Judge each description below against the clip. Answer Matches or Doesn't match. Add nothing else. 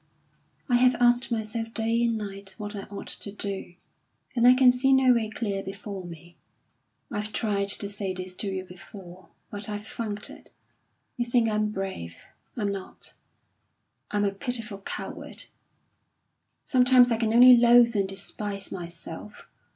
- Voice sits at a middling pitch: Doesn't match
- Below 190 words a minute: Matches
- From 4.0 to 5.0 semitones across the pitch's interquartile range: Doesn't match